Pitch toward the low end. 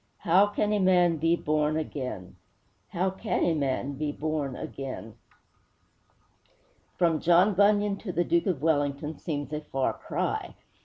No: medium, 160 Hz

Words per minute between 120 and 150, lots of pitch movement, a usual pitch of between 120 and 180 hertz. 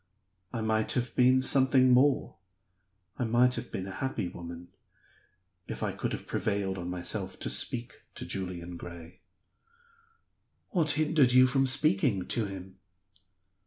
No: average, 140 wpm; wide, 5.7 semitones; low, 110 Hz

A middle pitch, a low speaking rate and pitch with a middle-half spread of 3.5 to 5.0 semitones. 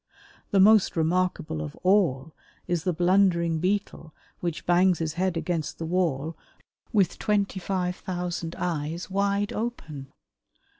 No: medium, 180 Hz; slow, 130 wpm; average, 2.9 semitones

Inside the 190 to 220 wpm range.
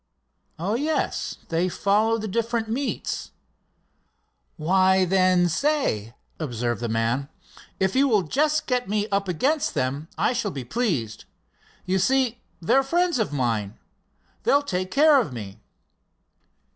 No: slow, 135 wpm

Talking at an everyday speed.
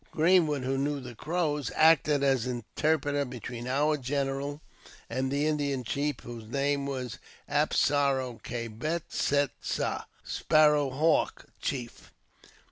No: slow, 130 wpm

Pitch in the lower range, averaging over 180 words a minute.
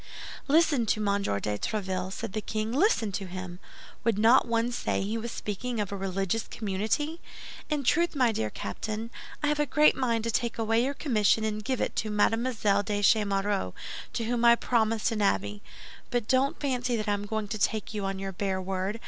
No: high, 220 Hz; average, 200 wpm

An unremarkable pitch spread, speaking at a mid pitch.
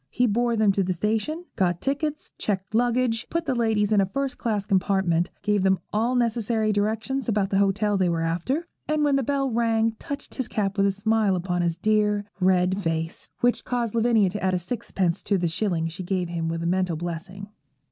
No: average, 4.2 semitones; high, 205 Hz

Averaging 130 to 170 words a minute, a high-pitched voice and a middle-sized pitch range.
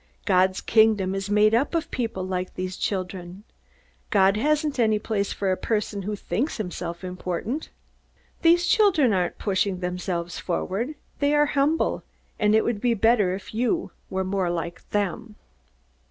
Yes: average, 155 wpm; high, 205 Hz; average, 4.2 semitones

